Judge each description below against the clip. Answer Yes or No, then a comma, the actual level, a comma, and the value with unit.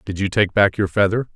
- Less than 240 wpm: No, fast, 265 wpm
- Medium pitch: No, low, 100 Hz